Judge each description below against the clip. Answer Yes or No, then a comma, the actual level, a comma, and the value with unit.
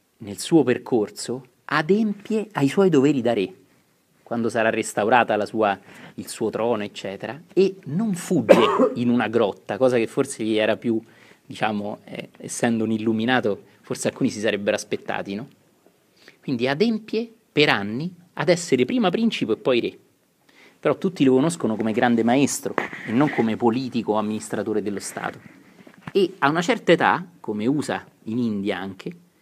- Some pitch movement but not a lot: No, wide, 8.1 semitones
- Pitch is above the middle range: No, low, 125 Hz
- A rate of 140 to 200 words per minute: Yes, average, 155 wpm